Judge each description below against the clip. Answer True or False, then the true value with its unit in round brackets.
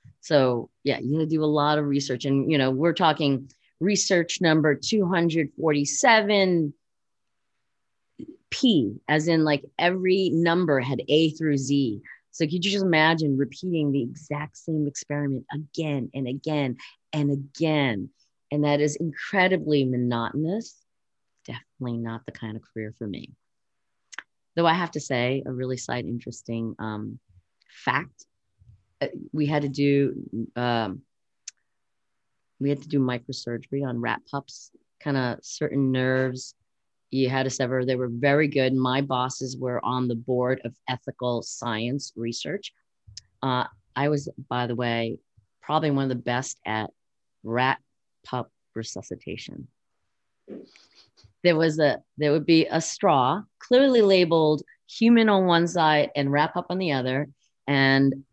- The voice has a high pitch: False (140 Hz)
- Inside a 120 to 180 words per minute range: True (140 wpm)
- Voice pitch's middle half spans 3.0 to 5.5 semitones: True (4.1 semitones)